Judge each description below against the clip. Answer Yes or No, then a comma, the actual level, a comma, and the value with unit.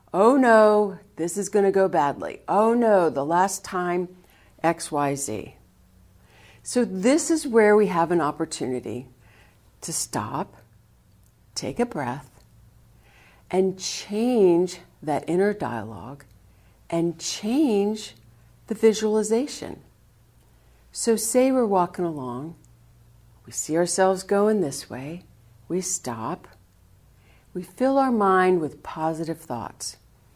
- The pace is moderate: No, slow, 110 wpm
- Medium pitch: Yes, medium, 165 Hz